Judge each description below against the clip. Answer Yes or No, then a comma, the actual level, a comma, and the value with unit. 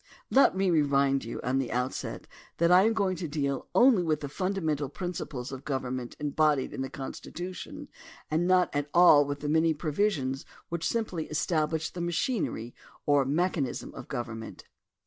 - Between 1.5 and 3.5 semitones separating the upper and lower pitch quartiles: No, average, 4.7 semitones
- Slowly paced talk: No, average, 165 wpm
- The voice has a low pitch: No, medium, 155 Hz